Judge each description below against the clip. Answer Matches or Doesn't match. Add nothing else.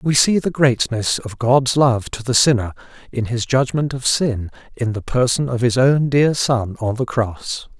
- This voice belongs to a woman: Doesn't match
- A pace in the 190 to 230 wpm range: Matches